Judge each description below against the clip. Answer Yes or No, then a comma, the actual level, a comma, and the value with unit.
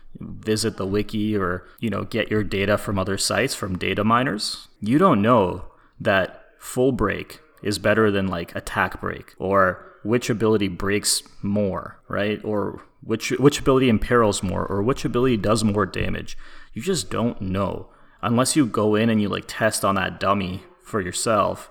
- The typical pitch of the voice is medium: No, low, 105 Hz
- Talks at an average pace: Yes, average, 170 wpm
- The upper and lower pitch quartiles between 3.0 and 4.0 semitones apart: No, narrow, 2.4 semitones